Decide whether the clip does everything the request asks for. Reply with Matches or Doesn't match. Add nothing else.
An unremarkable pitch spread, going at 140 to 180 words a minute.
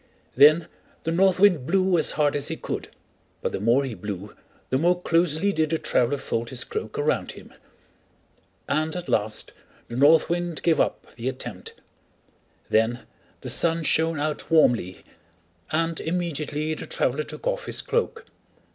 Matches